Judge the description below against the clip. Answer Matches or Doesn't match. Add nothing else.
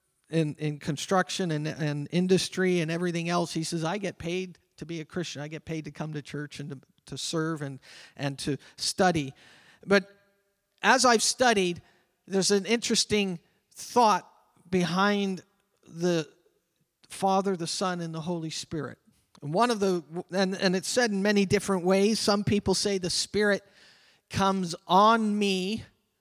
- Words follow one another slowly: Doesn't match